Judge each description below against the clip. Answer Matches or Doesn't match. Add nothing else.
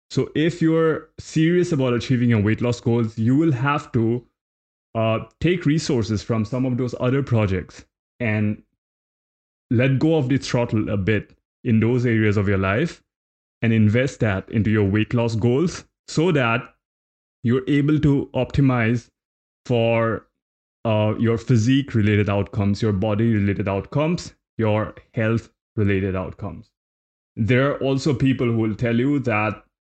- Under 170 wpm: Matches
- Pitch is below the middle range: Matches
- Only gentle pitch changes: Doesn't match